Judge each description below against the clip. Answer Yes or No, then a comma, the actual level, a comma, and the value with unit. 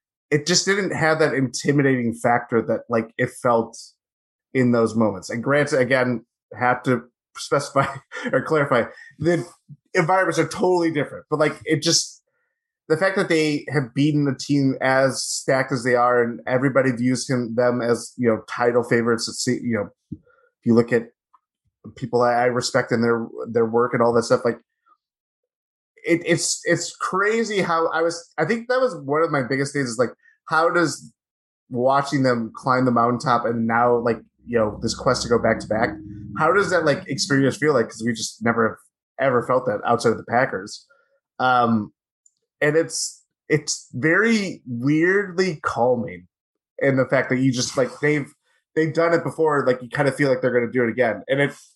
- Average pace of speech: Yes, average, 190 wpm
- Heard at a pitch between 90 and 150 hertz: Yes, low, 135 Hz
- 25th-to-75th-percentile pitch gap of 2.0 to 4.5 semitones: No, average, 5.2 semitones